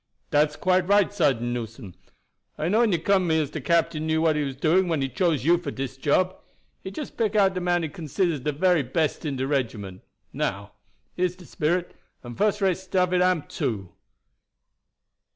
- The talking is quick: Yes, fast, 210 wpm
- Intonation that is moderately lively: Yes, average, 4.7 semitones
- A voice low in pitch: No, medium, 160 Hz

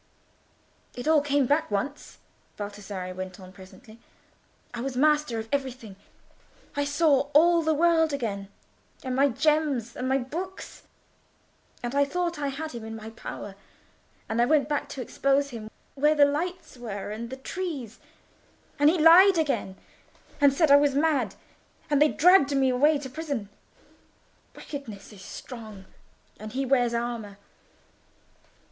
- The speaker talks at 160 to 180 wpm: No, average, 150 wpm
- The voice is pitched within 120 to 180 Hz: No, very high, 275 Hz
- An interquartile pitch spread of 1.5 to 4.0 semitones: No, average, 4.7 semitones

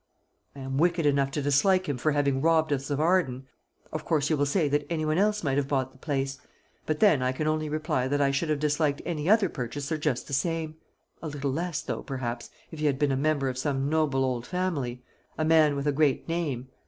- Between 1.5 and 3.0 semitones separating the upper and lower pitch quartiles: Yes, average, 2.7 semitones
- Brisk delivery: Yes, fast, 235 wpm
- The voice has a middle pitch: Yes, medium, 145 Hz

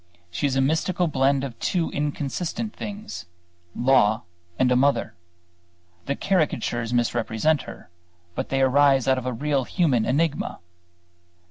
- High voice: No, low, 135 Hz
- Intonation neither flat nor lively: Yes, average, 3.7 semitones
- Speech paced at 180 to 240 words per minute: No, slow, 135 wpm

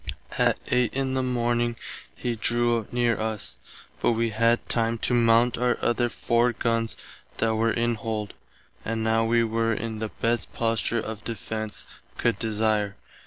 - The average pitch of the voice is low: Yes, low, 115 Hz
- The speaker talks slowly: No, average, 160 wpm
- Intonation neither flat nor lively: No, narrow, 1.1 semitones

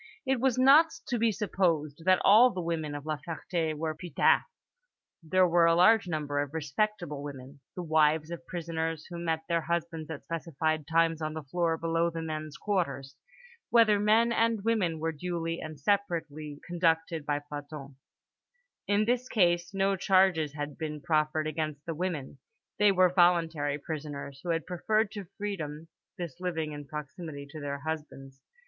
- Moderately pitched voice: Yes, medium, 165 Hz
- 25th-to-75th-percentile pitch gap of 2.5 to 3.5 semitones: Yes, average, 3.2 semitones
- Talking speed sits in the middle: Yes, average, 165 wpm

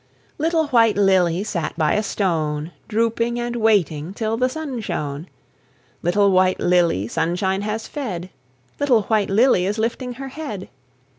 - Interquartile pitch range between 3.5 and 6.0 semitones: Yes, average, 4.9 semitones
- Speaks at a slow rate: No, average, 145 wpm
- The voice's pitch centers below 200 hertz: No, high, 205 Hz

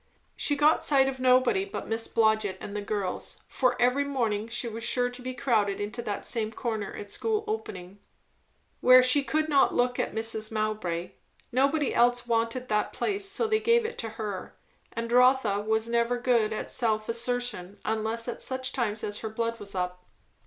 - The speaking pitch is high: Yes, high, 235 Hz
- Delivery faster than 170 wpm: Yes, average, 185 wpm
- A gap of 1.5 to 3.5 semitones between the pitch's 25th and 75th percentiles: Yes, average, 3.0 semitones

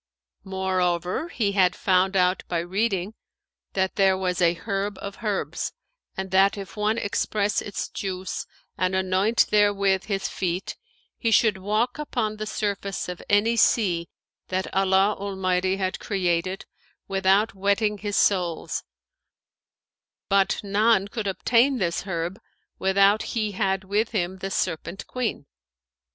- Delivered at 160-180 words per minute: No, slow, 135 wpm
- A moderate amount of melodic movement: No, narrow, 1.9 semitones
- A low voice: No, high, 195 Hz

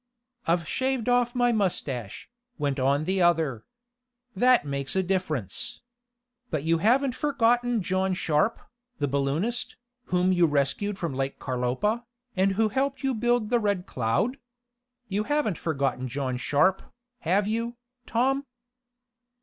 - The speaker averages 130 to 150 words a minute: Yes, slow, 135 wpm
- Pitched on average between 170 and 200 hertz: Yes, high, 190 Hz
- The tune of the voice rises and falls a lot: Yes, wide, 8.8 semitones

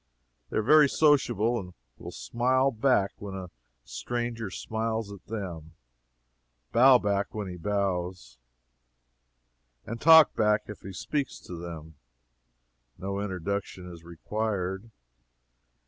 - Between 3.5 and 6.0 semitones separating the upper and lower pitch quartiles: Yes, average, 4.3 semitones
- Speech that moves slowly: Yes, slow, 115 wpm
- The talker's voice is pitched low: Yes, low, 100 Hz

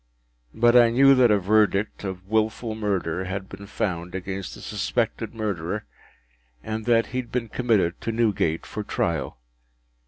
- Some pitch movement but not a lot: Yes, average, 3.4 semitones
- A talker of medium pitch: No, low, 105 Hz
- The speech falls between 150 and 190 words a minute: Yes, average, 155 wpm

